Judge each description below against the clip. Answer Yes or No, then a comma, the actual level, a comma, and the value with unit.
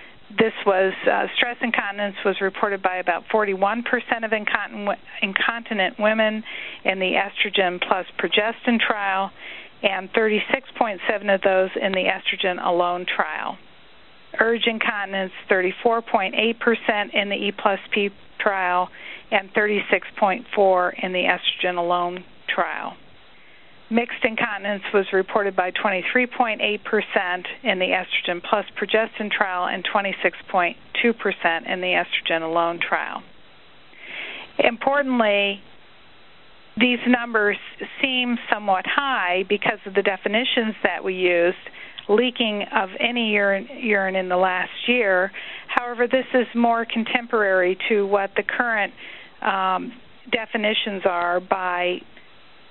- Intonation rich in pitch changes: No, average, 3.5 semitones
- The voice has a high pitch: Yes, high, 205 Hz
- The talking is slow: Yes, slow, 115 wpm